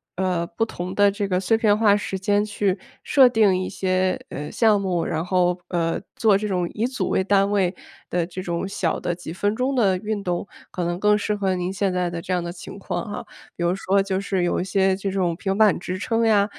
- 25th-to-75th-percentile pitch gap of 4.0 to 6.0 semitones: No, narrow, 2.4 semitones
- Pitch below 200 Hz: Yes, high, 190 Hz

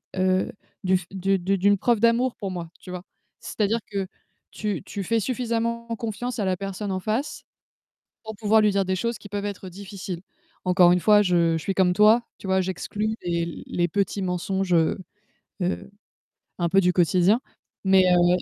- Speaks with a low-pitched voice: No, high, 195 Hz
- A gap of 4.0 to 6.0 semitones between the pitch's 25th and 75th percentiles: No, average, 2.7 semitones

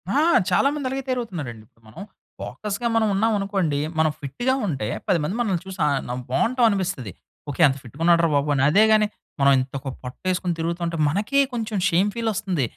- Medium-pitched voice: Yes, medium, 180 Hz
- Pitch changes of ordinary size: No, wide, 7.1 semitones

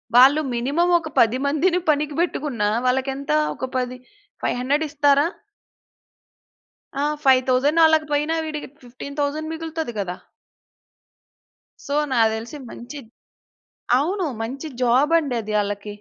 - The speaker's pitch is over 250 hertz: Yes, very high, 280 Hz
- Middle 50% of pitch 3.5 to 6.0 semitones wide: Yes, average, 3.8 semitones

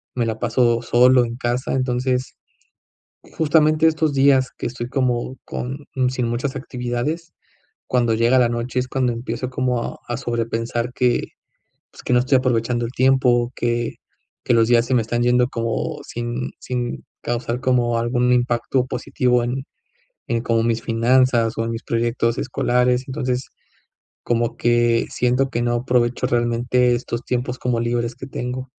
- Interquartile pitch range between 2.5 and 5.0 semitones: No, narrow, 1.4 semitones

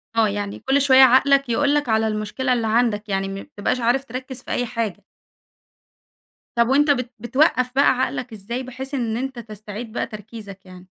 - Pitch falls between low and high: No, high, 235 Hz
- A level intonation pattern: No, average, 3.6 semitones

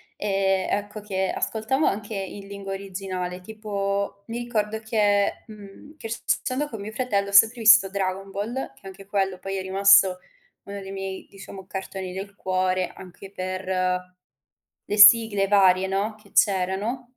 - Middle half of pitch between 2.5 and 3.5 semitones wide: No, narrow, 1.9 semitones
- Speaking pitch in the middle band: No, high, 200 Hz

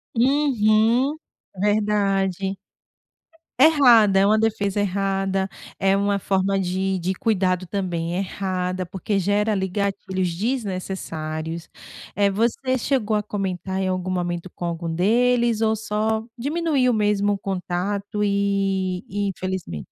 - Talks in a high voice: Yes, high, 195 Hz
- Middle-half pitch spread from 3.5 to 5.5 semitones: No, narrow, 2.5 semitones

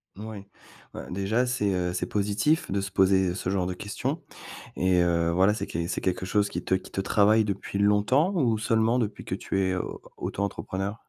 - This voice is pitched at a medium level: No, low, 100 Hz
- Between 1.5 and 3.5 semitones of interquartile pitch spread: Yes, average, 2.9 semitones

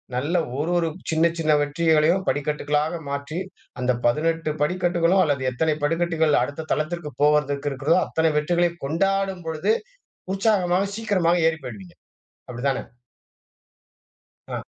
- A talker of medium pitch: Yes, medium, 160 Hz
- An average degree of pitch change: Yes, average, 3.1 semitones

